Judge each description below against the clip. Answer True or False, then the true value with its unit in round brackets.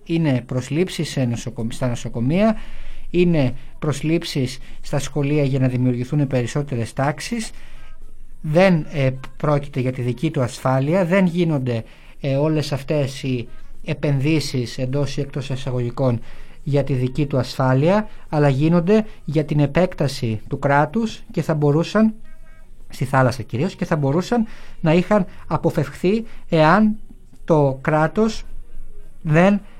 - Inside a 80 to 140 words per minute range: True (125 wpm)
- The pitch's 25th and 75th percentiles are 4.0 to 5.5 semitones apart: True (4.6 semitones)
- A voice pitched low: False (145 Hz)